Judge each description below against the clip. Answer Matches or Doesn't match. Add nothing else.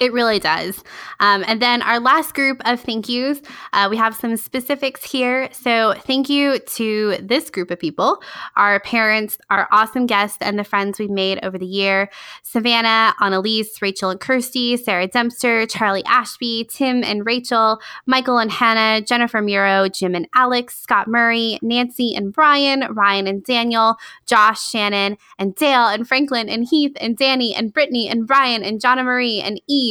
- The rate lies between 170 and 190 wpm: Matches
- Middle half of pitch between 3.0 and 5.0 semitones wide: Matches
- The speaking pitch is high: Matches